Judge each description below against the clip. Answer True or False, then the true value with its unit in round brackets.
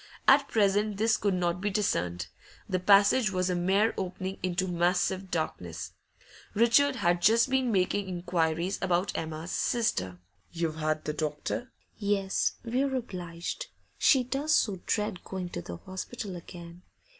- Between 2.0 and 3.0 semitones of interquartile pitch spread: False (3.8 semitones)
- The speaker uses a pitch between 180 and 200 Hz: True (185 Hz)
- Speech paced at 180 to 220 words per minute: False (145 wpm)